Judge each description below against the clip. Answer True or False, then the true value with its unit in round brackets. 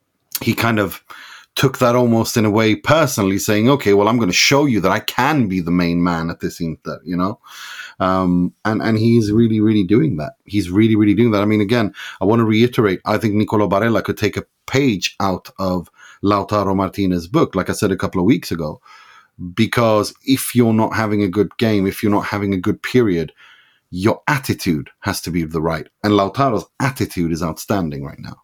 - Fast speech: True (215 wpm)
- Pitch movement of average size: True (3.2 semitones)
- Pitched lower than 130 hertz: True (105 Hz)